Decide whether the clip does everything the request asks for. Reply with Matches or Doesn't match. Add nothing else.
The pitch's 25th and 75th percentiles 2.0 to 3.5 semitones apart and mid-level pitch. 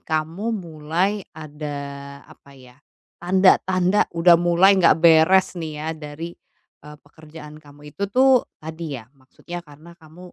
Matches